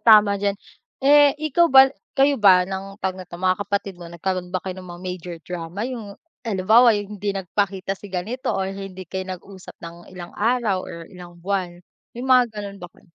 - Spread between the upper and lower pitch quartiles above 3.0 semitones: No, narrow, 2.5 semitones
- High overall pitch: Yes, high, 195 Hz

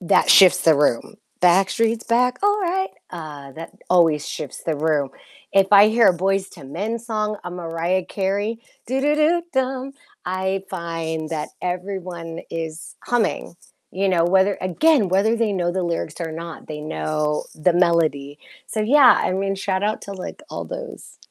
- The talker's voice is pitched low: No, medium, 185 Hz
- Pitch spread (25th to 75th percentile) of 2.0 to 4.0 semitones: No, average, 4.8 semitones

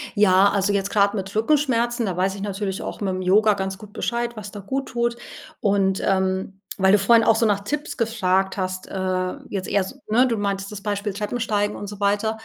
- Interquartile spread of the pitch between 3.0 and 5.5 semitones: No, narrow, 2.5 semitones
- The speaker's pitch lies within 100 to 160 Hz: No, high, 205 Hz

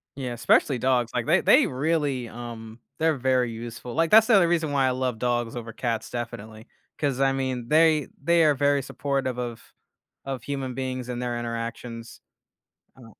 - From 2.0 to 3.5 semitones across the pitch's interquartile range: Yes, average, 3.0 semitones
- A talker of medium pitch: No, low, 125 Hz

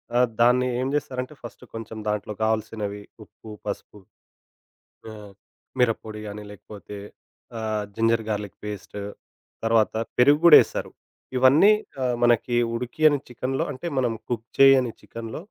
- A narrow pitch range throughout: No, average, 3.0 semitones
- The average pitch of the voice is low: Yes, low, 115 Hz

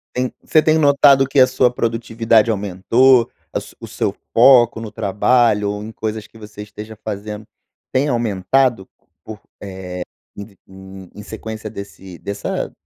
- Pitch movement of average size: Yes, average, 3.2 semitones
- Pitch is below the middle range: Yes, low, 110 Hz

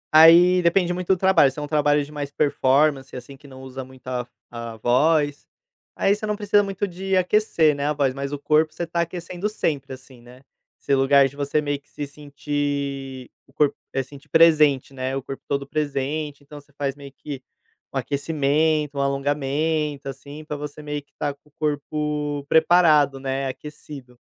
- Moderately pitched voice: Yes, medium, 145 Hz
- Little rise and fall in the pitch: Yes, narrow, 2.1 semitones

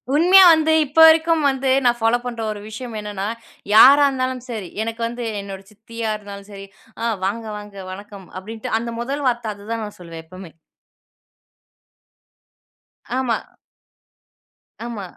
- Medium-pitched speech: No, high, 225 Hz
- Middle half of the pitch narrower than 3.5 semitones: No, average, 4.1 semitones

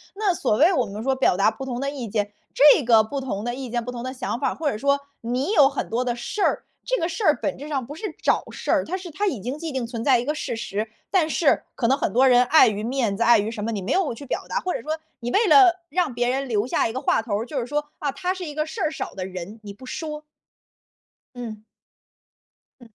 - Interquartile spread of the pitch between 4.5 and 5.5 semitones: Yes, average, 4.8 semitones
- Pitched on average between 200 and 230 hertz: No, very high, 260 Hz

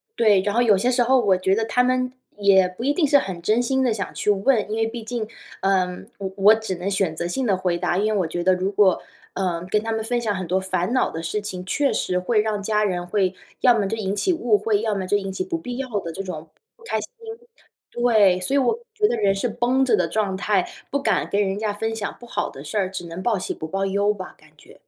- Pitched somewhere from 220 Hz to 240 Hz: No, high, 205 Hz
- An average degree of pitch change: Yes, average, 3.8 semitones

